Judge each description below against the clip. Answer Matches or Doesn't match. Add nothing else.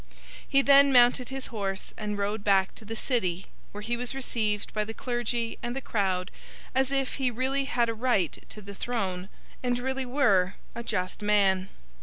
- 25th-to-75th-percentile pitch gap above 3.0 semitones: Matches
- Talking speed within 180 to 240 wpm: Matches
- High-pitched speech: Matches